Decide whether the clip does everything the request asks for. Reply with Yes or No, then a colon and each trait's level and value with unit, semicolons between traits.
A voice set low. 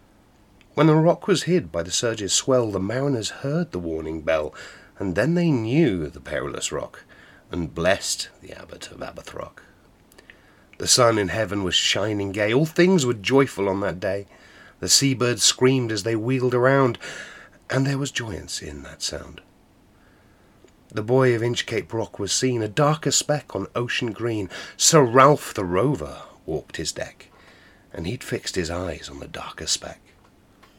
Yes: low, 115 Hz